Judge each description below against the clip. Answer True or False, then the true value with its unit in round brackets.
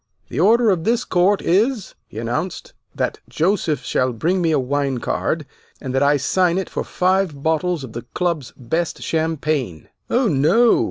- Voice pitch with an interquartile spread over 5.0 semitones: True (5.4 semitones)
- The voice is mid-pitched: True (160 Hz)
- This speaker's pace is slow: False (170 wpm)